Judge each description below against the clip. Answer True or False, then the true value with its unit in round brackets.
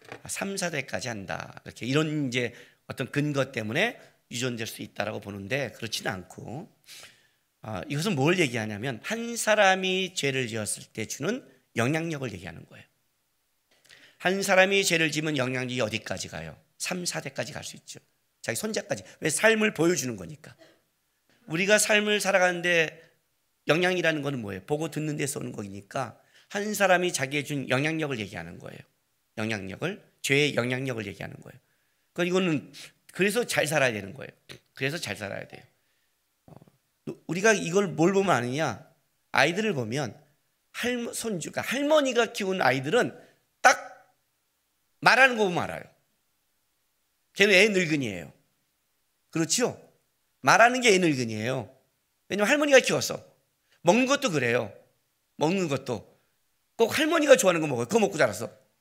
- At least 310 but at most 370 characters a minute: True (315 characters per minute)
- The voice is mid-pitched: True (150 Hz)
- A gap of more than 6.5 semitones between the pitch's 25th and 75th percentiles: True (8.5 semitones)